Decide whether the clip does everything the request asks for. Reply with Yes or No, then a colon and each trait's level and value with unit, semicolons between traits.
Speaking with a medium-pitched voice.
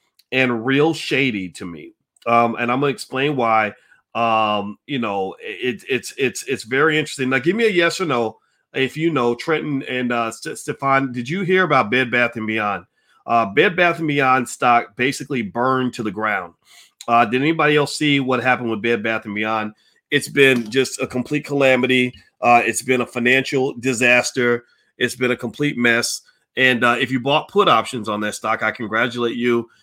No: low, 125 Hz